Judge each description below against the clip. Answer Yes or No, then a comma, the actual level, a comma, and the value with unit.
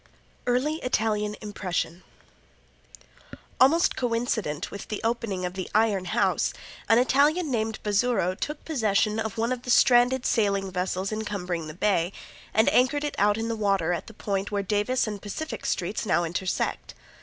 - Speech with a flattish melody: No, average, 3.9 semitones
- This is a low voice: No, high, 210 Hz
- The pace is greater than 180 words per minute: No, average, 155 wpm